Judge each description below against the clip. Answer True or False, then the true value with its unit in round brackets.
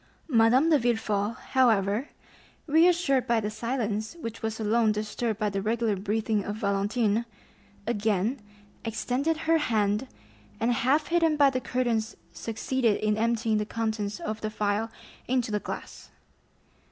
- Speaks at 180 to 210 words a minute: False (140 wpm)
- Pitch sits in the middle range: False (225 Hz)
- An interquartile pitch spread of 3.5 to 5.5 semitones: False (3.1 semitones)